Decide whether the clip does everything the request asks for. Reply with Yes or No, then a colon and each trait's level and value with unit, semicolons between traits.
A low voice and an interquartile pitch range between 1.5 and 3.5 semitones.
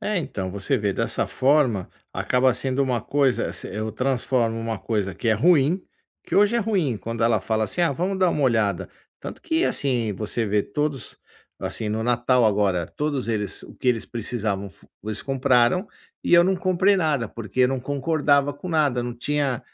No: low, 125 Hz; average, 5.1 semitones